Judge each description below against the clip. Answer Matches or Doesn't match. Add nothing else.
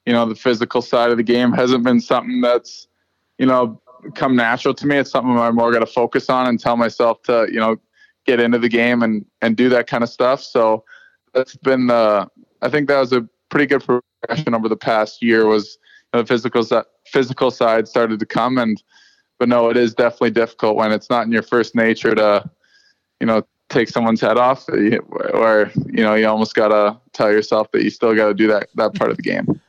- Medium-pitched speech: Doesn't match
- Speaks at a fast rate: Matches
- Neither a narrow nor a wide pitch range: Doesn't match